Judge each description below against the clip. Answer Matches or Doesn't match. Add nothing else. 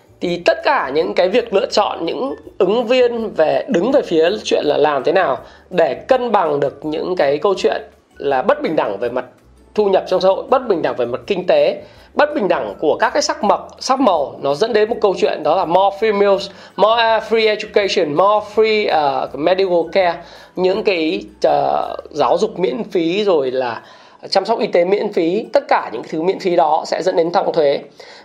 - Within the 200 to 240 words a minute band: Matches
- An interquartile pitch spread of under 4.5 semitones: Doesn't match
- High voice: Matches